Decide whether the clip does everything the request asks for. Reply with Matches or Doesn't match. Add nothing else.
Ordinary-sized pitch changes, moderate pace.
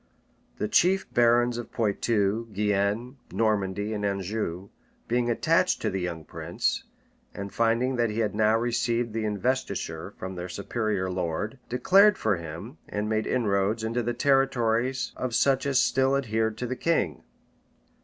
Matches